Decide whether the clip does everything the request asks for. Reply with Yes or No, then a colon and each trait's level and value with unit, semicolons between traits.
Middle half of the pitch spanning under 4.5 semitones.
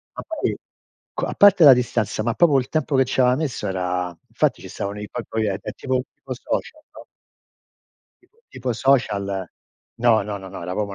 No: average, 5.0 semitones